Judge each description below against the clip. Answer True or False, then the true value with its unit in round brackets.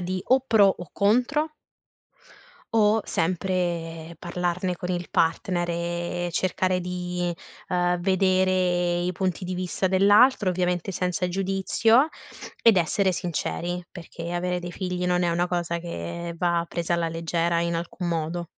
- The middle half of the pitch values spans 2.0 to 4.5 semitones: False (1.5 semitones)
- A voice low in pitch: False (180 Hz)